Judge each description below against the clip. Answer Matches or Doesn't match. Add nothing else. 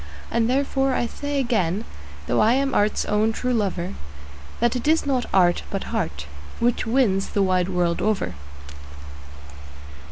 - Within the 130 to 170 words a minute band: Matches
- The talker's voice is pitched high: Matches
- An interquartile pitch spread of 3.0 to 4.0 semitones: Doesn't match